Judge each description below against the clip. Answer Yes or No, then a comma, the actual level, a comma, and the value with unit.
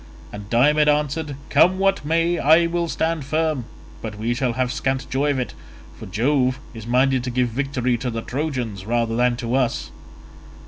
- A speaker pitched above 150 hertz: No, low, 130 Hz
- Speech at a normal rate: Yes, average, 180 wpm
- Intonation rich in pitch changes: No, average, 3.9 semitones